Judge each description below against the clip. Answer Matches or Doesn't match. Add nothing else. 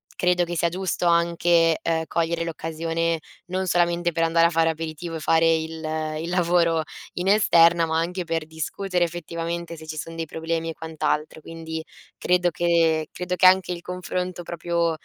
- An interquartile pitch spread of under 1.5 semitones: Matches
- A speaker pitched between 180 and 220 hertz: Doesn't match